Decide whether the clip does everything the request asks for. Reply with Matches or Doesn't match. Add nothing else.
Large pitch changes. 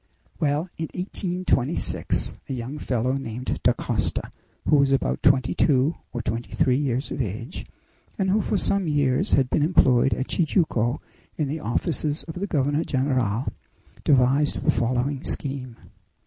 Doesn't match